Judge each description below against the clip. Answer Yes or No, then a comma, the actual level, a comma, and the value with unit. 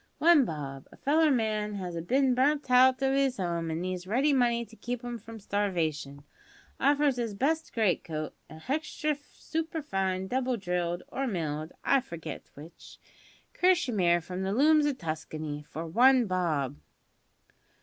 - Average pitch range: No, wide, 7.9 semitones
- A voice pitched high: Yes, high, 215 Hz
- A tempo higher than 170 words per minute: No, average, 155 wpm